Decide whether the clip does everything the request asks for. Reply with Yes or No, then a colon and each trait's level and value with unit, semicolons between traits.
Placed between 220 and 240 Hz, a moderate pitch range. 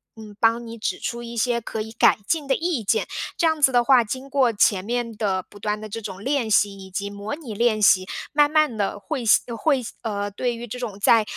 Yes: high, 230 Hz; average, 3.8 semitones